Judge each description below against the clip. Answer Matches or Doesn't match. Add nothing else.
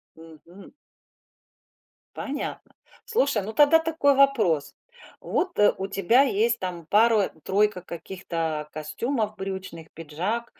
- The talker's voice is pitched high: Matches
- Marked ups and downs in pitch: Matches